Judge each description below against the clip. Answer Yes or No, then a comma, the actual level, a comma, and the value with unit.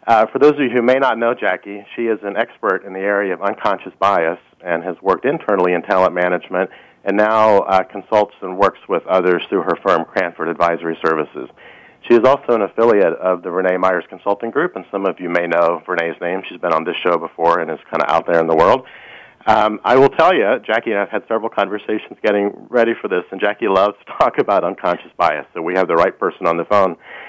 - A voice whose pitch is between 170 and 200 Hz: No, low, 100 Hz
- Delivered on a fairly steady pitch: No, average, 3.7 semitones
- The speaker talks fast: Yes, fast, 235 wpm